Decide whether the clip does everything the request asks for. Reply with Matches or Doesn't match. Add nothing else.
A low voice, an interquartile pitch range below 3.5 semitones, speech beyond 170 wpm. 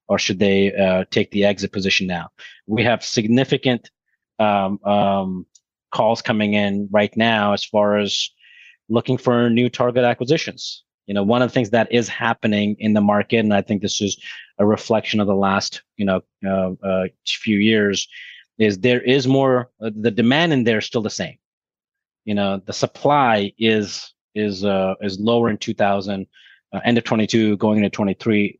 Matches